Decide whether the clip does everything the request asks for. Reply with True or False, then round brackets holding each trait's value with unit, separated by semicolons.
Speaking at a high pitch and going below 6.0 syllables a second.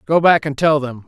False (145 Hz; 5.3 syllables/s)